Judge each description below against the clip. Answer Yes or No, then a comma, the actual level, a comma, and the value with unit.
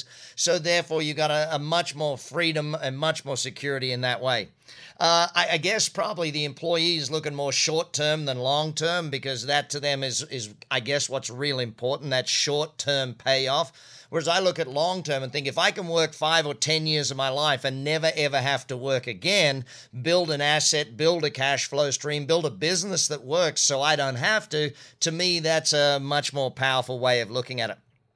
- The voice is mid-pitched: Yes, medium, 145 Hz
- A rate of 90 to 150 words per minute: No, fast, 205 wpm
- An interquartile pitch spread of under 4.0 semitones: Yes, average, 3.1 semitones